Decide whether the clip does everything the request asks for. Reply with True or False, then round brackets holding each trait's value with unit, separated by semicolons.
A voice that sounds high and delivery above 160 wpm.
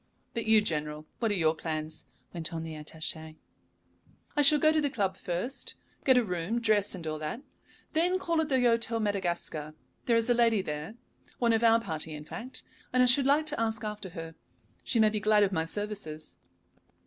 True (210 Hz; 200 wpm)